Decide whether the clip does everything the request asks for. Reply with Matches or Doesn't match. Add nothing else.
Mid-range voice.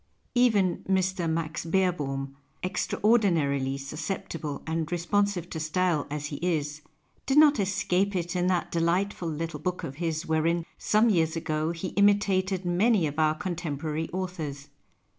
Matches